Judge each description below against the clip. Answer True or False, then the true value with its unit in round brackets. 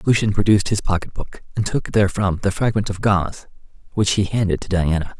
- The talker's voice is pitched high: False (100 Hz)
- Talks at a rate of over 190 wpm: False (185 wpm)